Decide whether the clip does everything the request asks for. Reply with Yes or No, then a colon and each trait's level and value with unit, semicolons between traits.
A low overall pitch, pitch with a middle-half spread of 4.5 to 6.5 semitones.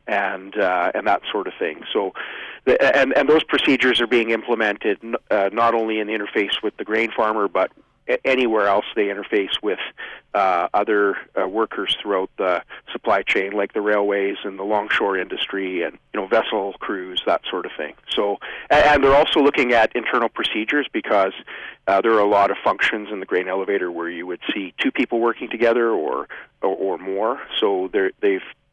Yes: low, 115 Hz; wide, 5.6 semitones